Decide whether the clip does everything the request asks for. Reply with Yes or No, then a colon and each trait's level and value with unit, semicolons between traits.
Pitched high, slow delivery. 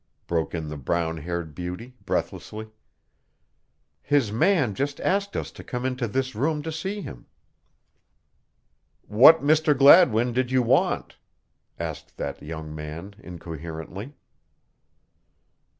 No: low, 110 Hz; slow, 120 wpm